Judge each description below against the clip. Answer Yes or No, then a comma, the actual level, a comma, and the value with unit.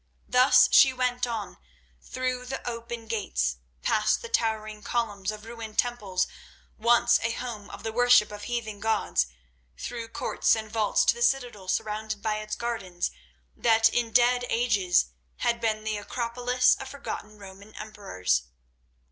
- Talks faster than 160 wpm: No, average, 150 wpm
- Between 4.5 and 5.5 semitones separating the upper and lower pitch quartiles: No, narrow, 2.5 semitones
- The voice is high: Yes, high, 225 Hz